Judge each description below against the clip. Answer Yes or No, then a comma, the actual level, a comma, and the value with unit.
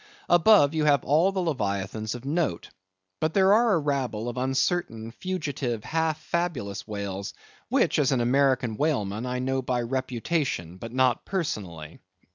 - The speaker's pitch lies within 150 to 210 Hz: No, low, 130 Hz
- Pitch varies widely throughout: Yes, wide, 6.0 semitones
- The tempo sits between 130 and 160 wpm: Yes, average, 150 wpm